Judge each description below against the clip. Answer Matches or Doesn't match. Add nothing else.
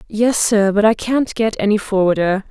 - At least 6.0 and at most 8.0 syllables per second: Doesn't match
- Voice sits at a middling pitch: Doesn't match